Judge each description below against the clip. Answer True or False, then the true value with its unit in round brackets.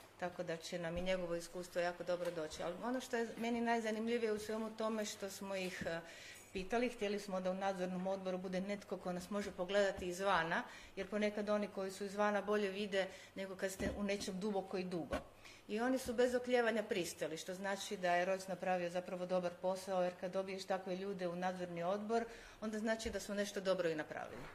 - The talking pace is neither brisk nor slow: False (205 wpm)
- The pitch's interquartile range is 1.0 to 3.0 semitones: True (2.5 semitones)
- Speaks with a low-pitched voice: False (195 Hz)